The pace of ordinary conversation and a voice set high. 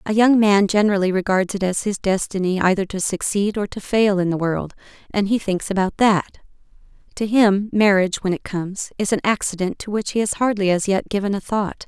No: fast, 210 wpm; high, 200 Hz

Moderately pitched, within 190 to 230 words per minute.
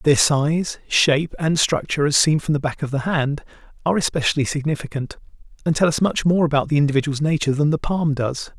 Yes: medium, 150 Hz; fast, 205 wpm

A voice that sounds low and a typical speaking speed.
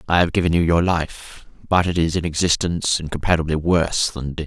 No: very low, 85 Hz; fast, 215 wpm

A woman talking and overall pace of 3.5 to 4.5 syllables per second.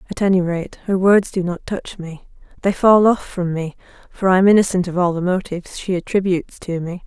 No: female; 5.6 syllables/s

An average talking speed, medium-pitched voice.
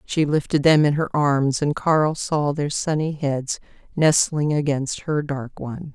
Yes: average, 170 wpm; medium, 145 Hz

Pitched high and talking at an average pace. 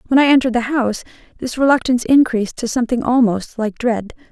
Yes: high, 240 Hz; average, 180 wpm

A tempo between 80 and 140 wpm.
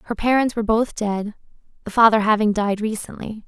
No: average, 175 wpm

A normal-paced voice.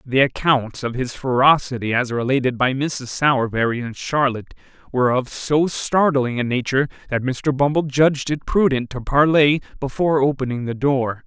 Yes: average, 160 wpm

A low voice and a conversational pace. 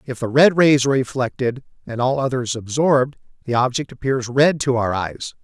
Yes: low, 130 Hz; average, 190 wpm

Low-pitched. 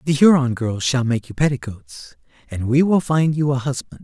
Yes: low, 130 Hz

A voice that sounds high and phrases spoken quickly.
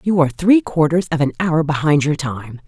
No: medium, 160 Hz; fast, 225 wpm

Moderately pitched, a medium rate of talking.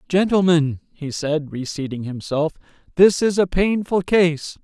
No: medium, 165 Hz; slow, 130 wpm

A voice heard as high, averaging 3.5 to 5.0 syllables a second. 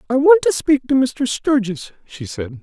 Yes: high, 225 Hz; 4.5 syllables/s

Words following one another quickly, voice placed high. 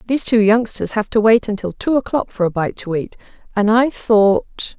Yes: fast, 215 wpm; high, 215 Hz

